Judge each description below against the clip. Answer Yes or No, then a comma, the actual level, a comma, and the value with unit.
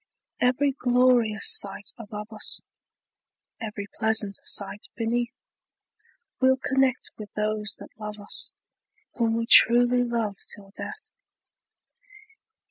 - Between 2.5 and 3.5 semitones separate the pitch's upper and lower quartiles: Yes, average, 2.8 semitones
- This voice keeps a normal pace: No, slow, 105 wpm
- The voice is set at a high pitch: Yes, high, 225 Hz